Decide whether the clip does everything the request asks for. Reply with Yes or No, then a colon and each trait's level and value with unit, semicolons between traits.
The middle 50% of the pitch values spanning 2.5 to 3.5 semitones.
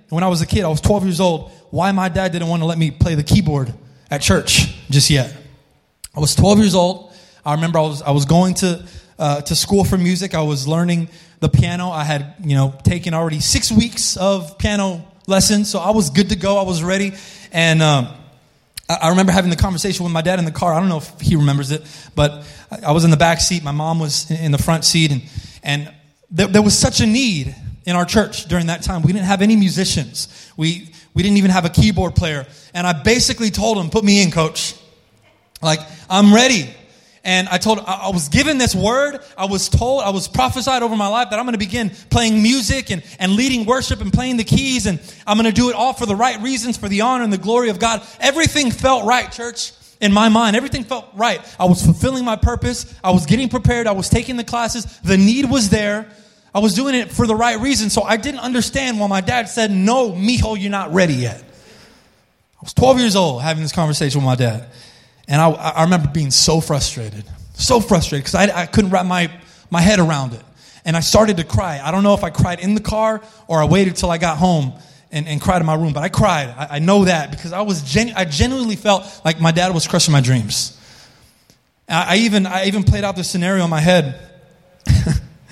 No: average, 5.2 semitones